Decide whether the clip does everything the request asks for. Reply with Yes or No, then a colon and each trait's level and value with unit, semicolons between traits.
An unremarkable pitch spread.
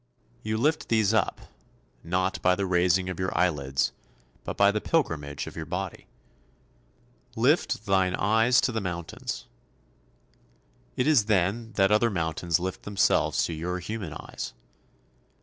Yes: average, 3.8 semitones